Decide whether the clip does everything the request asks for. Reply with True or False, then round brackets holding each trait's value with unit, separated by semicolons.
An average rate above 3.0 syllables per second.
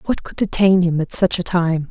True (5.1 syllables/s)